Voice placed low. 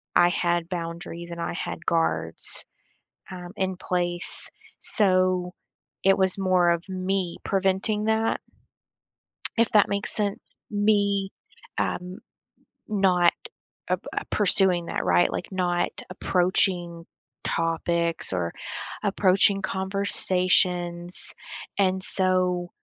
No: medium, 185 Hz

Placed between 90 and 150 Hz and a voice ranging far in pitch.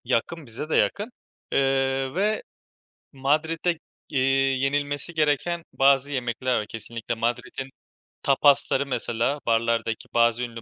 No: low, 135 Hz; average, 3.4 semitones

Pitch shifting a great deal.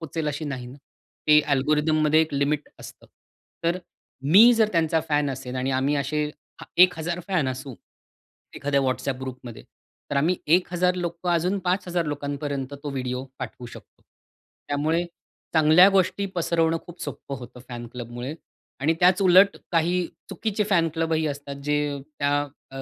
No: average, 3.7 semitones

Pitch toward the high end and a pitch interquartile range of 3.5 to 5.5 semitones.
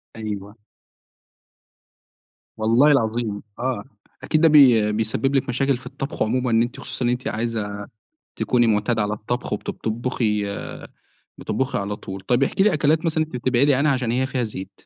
No: low, 120 Hz; average, 3.8 semitones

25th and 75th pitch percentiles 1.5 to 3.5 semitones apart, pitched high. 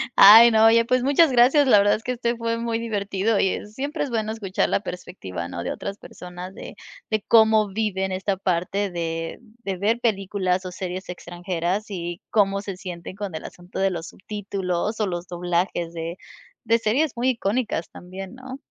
No: average, 4.0 semitones; high, 200 Hz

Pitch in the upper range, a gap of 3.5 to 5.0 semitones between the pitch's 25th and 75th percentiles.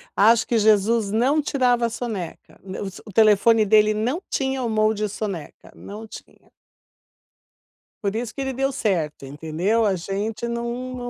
No: high, 220 Hz; average, 3.0 semitones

